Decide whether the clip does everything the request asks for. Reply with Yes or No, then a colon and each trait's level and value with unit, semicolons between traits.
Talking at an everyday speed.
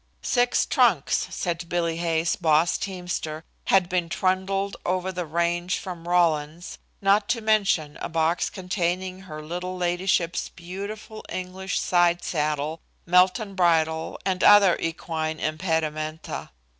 No: slow, 120 wpm